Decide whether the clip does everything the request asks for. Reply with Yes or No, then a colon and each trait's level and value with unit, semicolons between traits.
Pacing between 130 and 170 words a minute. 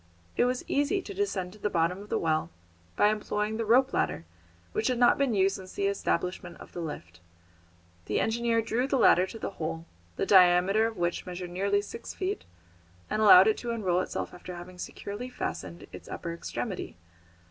No: average, 190 wpm